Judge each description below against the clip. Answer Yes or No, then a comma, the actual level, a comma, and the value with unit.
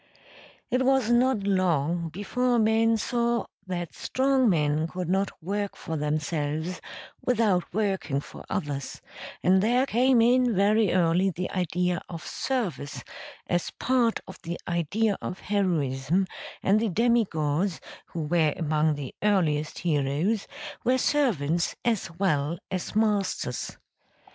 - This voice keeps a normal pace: No, slow, 130 wpm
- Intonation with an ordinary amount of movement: No, wide, 5.8 semitones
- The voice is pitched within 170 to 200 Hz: Yes, medium, 185 Hz